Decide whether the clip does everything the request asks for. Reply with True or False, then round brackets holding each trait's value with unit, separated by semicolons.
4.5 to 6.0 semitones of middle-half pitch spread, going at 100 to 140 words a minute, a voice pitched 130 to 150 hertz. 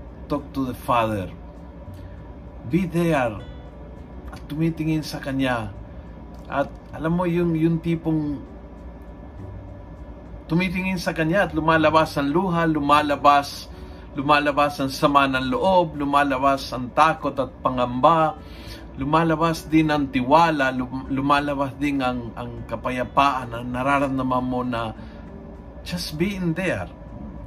True (5.1 semitones; 110 wpm; 140 Hz)